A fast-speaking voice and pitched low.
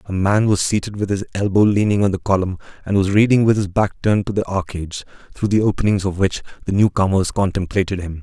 Yes: fast, 225 wpm; low, 100 Hz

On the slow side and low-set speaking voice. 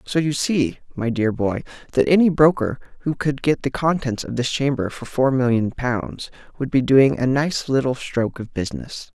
No: average, 195 wpm; low, 130 Hz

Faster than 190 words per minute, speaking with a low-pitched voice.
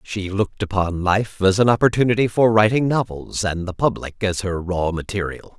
No: average, 185 wpm; low, 100 Hz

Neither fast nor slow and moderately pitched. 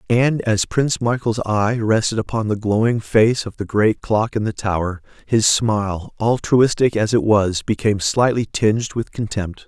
No: average, 175 wpm; low, 110 Hz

